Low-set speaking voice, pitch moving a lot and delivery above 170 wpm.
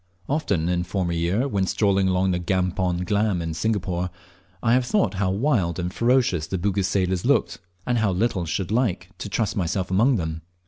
No: very low, 95 Hz; average, 3.3 semitones; average, 185 wpm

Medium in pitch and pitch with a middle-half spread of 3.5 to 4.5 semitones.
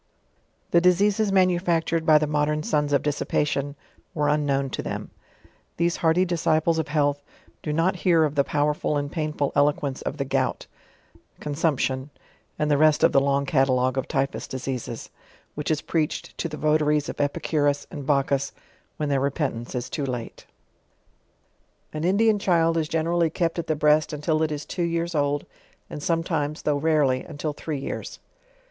No: medium, 150 Hz; narrow, 2.4 semitones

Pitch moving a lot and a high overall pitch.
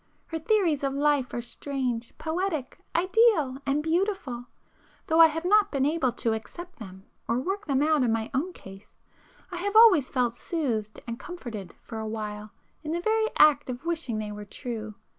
Yes: wide, 6.6 semitones; very high, 280 Hz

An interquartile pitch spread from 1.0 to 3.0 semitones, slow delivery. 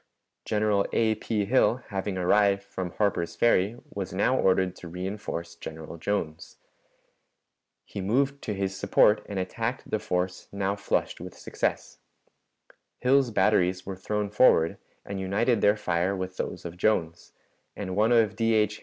No: average, 2.7 semitones; average, 150 wpm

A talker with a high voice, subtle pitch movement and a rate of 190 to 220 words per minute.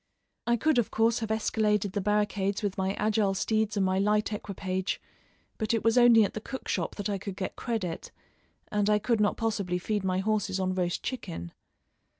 Yes: high, 210 Hz; narrow, 2.3 semitones; average, 195 wpm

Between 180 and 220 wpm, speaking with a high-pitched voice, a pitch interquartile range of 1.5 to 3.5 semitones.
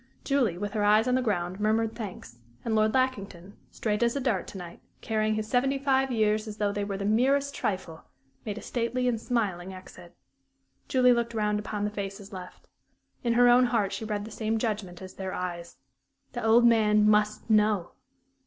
Yes: average, 200 wpm; high, 215 Hz; average, 2.9 semitones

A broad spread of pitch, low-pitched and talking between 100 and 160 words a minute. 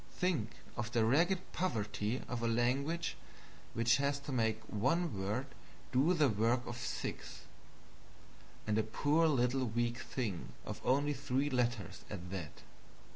No: average, 4.2 semitones; low, 120 Hz; average, 140 wpm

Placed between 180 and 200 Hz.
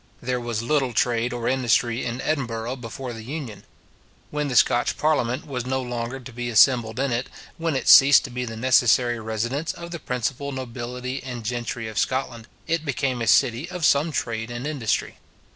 No: low, 125 Hz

